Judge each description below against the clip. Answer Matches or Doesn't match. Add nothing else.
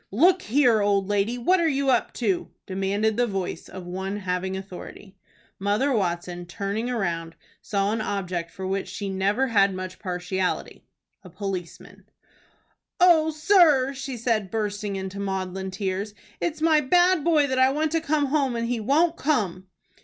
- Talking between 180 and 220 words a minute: Doesn't match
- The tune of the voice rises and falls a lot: Matches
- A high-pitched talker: Matches